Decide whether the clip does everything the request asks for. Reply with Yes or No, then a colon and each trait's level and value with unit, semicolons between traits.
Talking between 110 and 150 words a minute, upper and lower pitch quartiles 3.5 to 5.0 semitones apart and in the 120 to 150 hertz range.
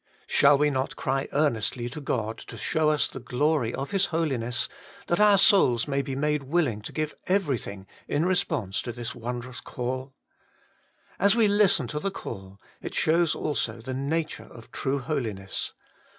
No: average, 165 wpm; average, 4.7 semitones; medium, 140 Hz